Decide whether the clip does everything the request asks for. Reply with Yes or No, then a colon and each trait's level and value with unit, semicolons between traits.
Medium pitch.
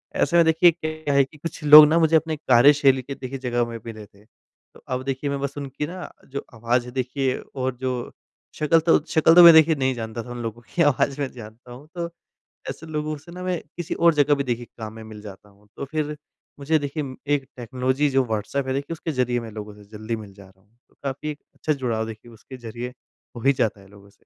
No: low, 130 Hz